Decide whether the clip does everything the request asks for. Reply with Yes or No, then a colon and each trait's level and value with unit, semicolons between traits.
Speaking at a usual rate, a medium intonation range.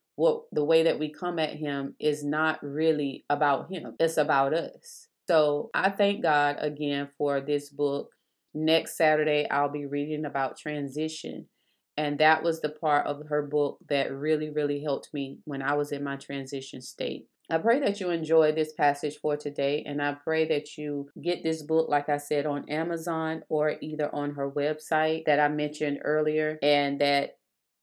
No: average, 180 wpm; narrow, 1.5 semitones